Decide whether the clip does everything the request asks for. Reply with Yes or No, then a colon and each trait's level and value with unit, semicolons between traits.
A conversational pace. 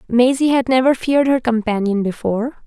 Yes: average, 160 wpm